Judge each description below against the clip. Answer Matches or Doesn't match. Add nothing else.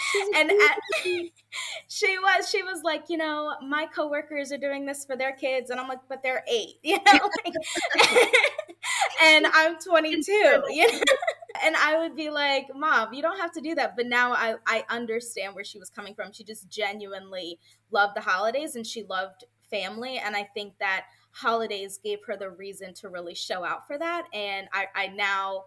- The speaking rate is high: Doesn't match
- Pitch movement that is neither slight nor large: Doesn't match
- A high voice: Matches